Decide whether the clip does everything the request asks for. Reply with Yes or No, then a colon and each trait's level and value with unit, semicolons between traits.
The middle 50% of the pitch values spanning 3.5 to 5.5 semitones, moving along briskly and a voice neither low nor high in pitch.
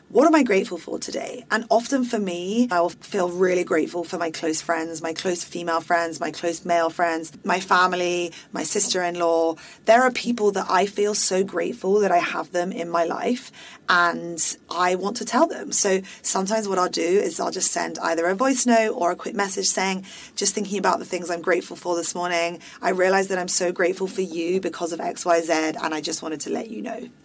No: average, 3.0 semitones; fast, 215 wpm; medium, 180 Hz